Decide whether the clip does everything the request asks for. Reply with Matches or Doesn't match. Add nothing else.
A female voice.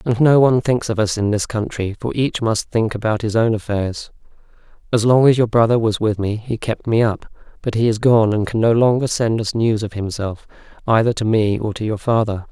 Doesn't match